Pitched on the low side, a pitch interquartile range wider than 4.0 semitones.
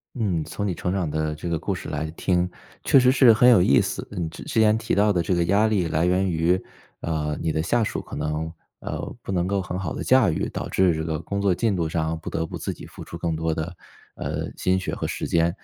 No: very low, 90 Hz; average, 3.6 semitones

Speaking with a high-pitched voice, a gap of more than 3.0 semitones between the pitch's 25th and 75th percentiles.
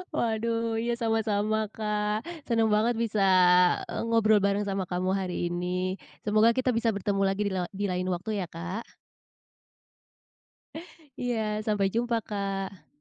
No: high, 210 Hz; average, 2.7 semitones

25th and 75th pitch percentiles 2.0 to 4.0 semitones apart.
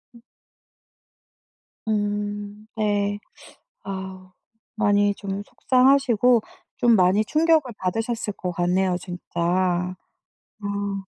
Yes: average, 2.8 semitones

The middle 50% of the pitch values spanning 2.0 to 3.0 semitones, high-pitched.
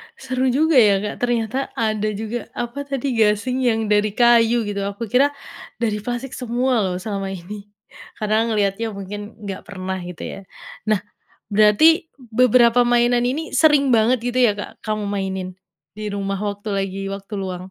No: average, 3.4 semitones; high, 220 Hz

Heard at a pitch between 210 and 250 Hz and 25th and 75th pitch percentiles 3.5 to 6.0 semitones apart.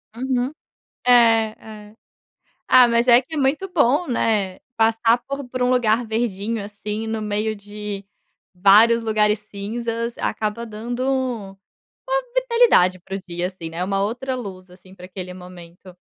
Yes: high, 220 Hz; average, 3.9 semitones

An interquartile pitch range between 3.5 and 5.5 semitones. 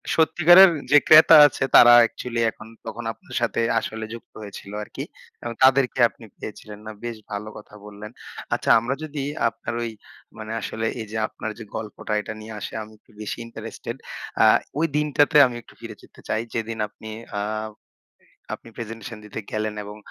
No: average, 2.8 semitones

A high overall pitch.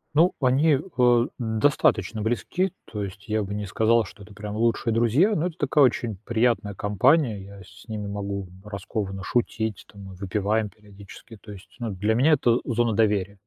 No: low, 110 Hz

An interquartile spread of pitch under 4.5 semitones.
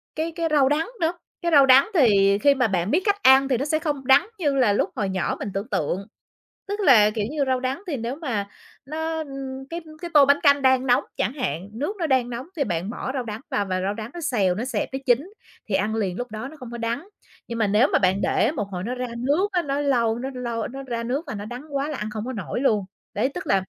No: average, 5.0 semitones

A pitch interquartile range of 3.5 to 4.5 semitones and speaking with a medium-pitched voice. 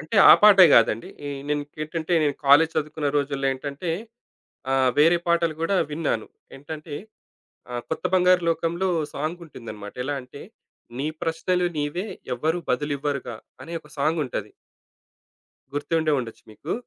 No: average, 3.0 semitones; medium, 155 Hz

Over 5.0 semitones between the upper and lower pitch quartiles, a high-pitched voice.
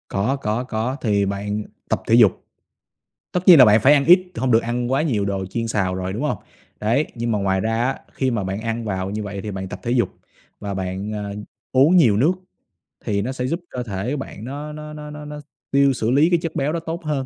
No: wide, 5.5 semitones; low, 120 Hz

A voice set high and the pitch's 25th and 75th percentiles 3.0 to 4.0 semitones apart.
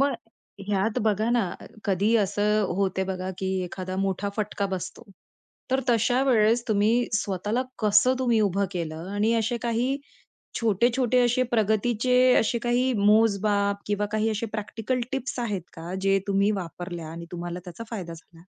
Yes: high, 210 Hz; average, 3.3 semitones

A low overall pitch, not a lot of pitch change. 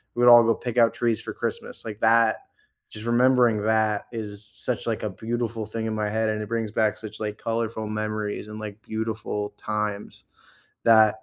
Yes: low, 110 Hz; narrow, 1.3 semitones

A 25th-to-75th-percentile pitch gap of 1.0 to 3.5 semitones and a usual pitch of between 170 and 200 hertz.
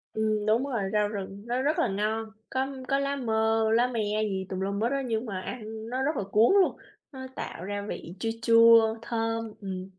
No: average, 2.9 semitones; high, 225 Hz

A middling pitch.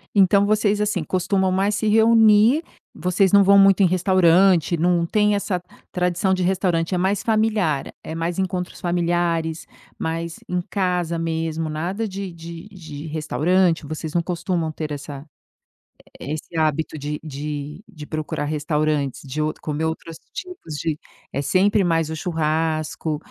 Yes: medium, 170 Hz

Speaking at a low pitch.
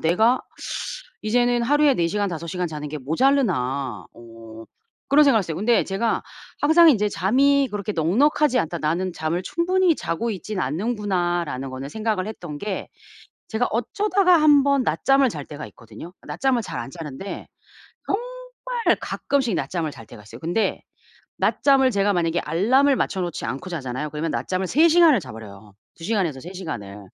No: high, 190 Hz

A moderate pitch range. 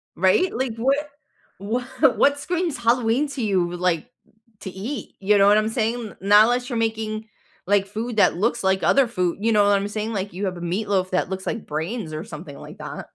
Yes: average, 3.8 semitones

